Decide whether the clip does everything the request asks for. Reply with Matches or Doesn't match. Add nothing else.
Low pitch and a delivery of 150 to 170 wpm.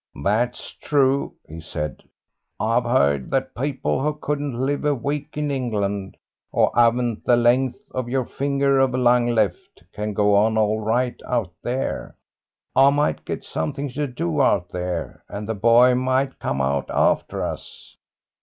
Matches